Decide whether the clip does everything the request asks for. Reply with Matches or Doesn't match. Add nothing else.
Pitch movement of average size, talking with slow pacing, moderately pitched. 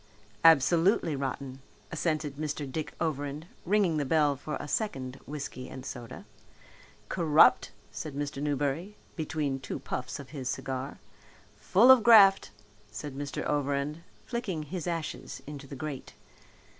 Matches